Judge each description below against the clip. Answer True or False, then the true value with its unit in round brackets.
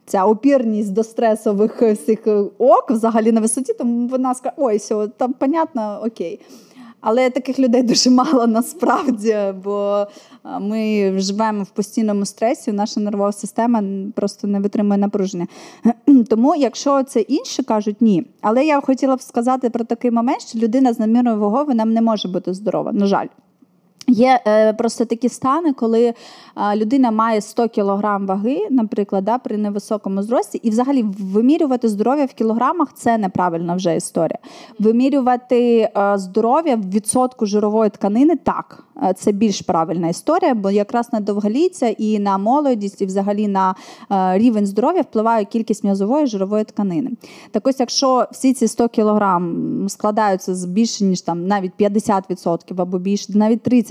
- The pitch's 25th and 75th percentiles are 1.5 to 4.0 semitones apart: True (3.5 semitones)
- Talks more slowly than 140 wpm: False (145 wpm)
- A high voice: True (225 Hz)